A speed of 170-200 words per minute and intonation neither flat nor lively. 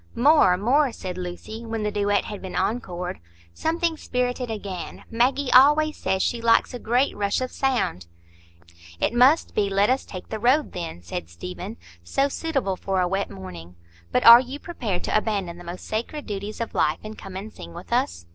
No: average, 185 wpm; wide, 5.7 semitones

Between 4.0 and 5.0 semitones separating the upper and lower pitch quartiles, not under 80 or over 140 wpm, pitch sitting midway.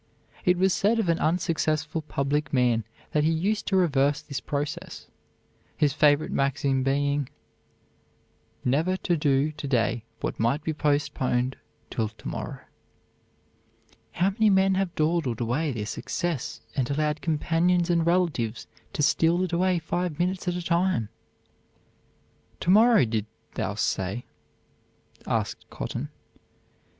Yes: average, 4.5 semitones; slow, 135 wpm; medium, 155 Hz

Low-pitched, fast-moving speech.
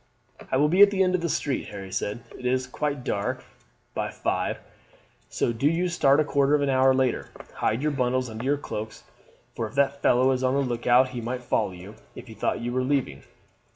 Yes: low, 130 Hz; fast, 225 wpm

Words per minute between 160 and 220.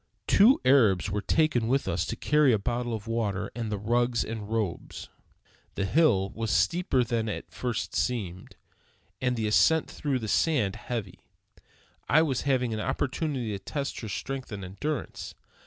Yes: average, 170 wpm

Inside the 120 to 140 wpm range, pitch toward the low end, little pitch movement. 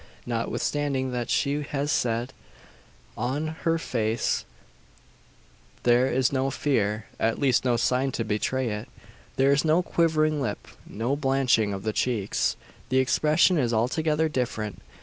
No: slow, 135 wpm; low, 130 Hz; average, 4.1 semitones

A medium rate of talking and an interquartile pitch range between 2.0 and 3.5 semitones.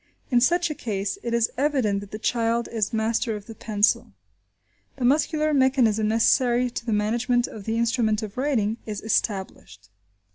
Yes: average, 170 wpm; average, 2.8 semitones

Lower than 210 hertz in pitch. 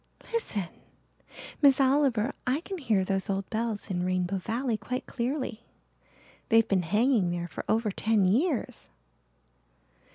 No: high, 225 Hz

